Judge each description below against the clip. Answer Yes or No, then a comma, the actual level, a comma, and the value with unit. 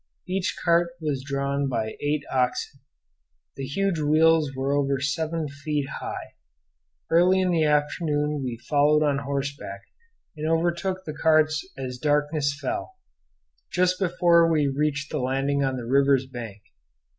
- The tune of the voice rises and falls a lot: No, average, 2.9 semitones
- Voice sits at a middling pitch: Yes, medium, 150 Hz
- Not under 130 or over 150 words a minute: Yes, average, 140 wpm